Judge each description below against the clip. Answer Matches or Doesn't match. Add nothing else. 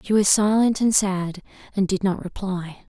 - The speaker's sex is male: Doesn't match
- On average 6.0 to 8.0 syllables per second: Doesn't match